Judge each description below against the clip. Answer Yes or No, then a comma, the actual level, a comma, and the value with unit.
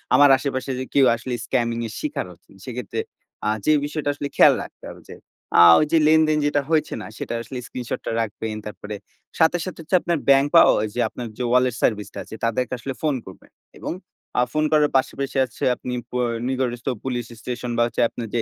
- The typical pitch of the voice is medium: No, low, 130 Hz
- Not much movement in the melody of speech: No, average, 3.8 semitones